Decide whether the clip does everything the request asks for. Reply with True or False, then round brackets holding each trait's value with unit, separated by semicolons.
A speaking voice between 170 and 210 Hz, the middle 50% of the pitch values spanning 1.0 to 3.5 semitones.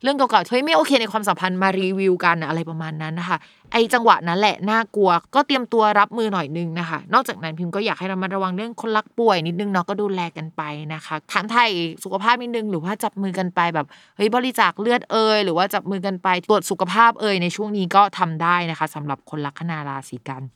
False (190 Hz; 4.4 semitones)